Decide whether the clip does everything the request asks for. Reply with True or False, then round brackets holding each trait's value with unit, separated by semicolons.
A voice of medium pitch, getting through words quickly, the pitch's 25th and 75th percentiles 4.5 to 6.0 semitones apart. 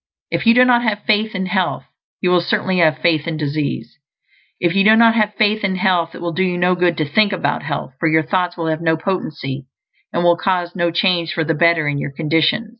False (175 Hz; 240 wpm; 3.3 semitones)